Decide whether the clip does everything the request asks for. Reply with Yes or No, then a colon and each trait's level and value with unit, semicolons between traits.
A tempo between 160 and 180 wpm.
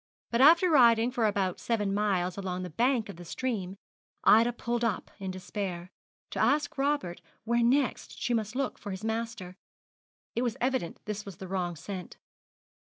Yes: average, 170 wpm